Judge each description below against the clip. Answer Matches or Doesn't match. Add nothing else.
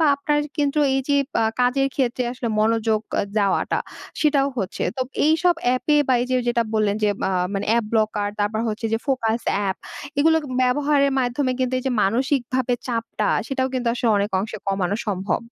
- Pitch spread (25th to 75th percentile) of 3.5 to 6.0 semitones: Matches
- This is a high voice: Matches